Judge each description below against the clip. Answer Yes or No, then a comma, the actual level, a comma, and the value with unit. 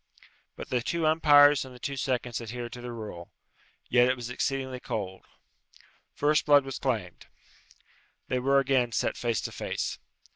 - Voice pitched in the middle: No, low, 125 Hz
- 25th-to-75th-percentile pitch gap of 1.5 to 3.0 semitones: Yes, narrow, 2.6 semitones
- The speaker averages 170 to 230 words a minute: No, average, 160 wpm